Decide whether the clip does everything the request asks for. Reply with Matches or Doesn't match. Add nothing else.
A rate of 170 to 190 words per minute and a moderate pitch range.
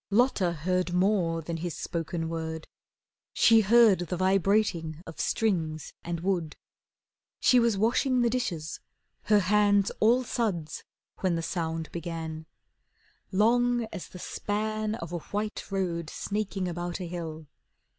Doesn't match